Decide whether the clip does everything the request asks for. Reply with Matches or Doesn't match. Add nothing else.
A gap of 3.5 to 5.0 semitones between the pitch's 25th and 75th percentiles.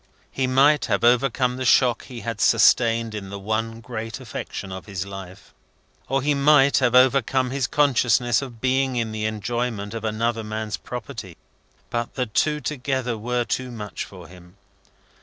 Doesn't match